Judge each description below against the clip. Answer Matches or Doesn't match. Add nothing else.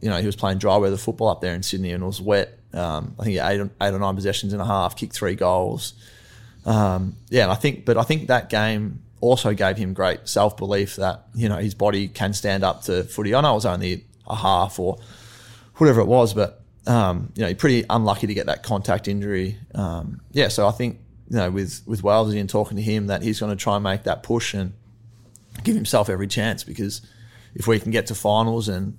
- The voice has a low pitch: Matches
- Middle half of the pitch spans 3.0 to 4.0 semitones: Doesn't match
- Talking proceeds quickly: Matches